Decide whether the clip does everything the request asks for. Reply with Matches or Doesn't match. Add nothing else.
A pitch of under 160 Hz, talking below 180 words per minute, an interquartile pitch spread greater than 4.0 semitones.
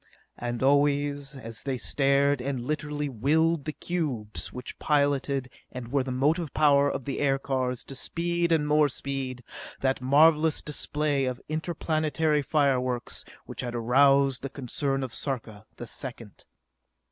Doesn't match